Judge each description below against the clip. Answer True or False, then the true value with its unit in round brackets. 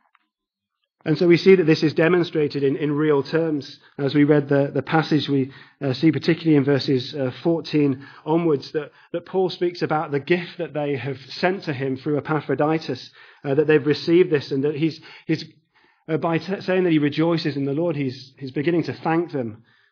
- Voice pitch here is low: False (150 Hz)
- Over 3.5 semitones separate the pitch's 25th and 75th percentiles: False (2.8 semitones)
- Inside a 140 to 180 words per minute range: False (200 wpm)